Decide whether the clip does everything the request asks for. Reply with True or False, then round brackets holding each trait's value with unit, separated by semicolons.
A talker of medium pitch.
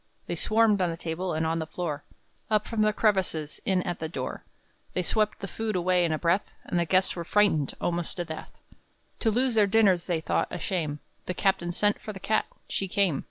True (180 Hz)